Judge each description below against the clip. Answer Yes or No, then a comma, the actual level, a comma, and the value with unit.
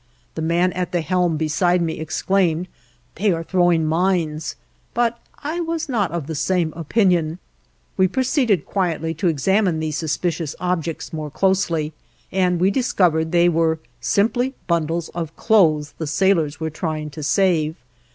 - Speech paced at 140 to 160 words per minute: Yes, average, 150 wpm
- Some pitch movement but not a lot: Yes, average, 3.0 semitones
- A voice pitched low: No, medium, 170 Hz